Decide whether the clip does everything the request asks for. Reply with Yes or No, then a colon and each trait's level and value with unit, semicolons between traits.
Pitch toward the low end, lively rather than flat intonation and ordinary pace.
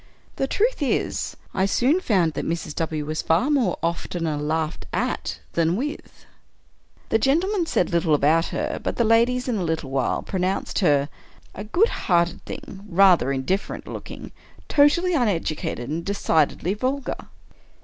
No: medium, 185 Hz; wide, 7.6 semitones; average, 150 wpm